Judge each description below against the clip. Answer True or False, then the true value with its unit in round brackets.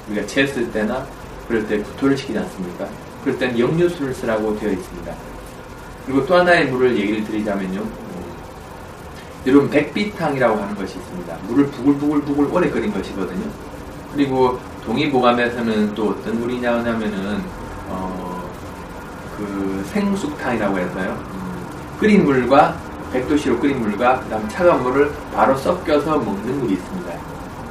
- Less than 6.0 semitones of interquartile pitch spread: True (5.2 semitones)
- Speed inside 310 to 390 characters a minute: True (330 characters per minute)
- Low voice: True (120 Hz)